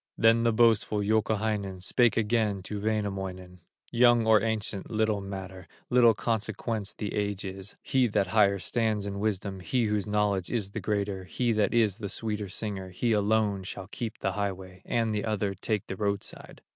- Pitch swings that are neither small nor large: No, narrow, 2.1 semitones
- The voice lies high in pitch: No, low, 105 Hz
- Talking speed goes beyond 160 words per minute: Yes, average, 170 wpm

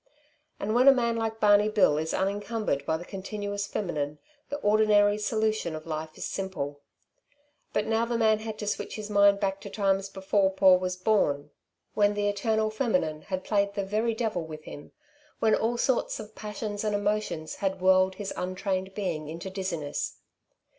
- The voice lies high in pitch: Yes, high, 200 Hz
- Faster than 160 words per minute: Yes, average, 175 wpm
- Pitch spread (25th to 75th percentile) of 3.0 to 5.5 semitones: No, narrow, 2.6 semitones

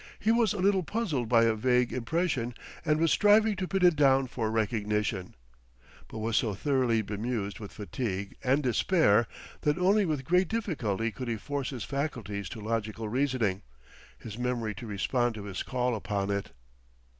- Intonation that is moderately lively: No, wide, 5.8 semitones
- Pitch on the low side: Yes, low, 125 Hz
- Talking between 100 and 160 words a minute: No, average, 170 wpm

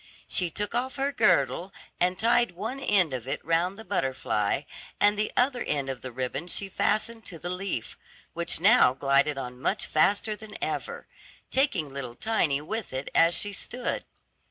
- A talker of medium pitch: Yes, medium, 180 Hz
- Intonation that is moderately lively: No, wide, 7.9 semitones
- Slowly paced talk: No, average, 175 wpm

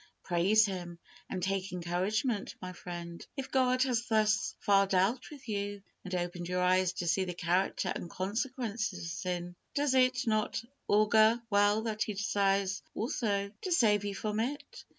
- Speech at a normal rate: Yes, average, 165 wpm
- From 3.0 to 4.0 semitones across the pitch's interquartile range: Yes, average, 3.4 semitones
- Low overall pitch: No, high, 200 Hz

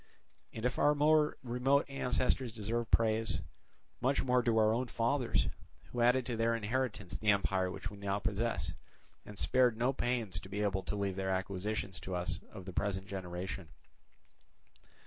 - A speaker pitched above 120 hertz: No, low, 110 Hz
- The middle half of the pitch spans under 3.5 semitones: No, average, 4.2 semitones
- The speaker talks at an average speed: Yes, average, 165 wpm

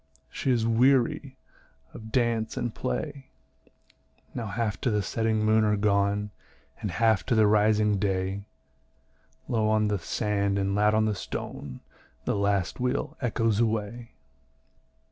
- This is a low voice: Yes, low, 110 Hz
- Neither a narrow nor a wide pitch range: No, narrow, 2.3 semitones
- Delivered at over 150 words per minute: No, average, 140 wpm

